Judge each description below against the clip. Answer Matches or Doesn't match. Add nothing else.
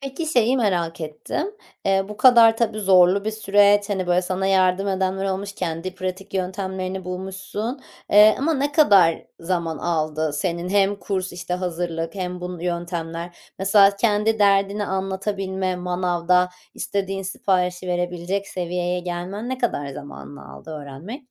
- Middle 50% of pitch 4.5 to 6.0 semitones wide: Doesn't match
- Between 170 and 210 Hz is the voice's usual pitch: Matches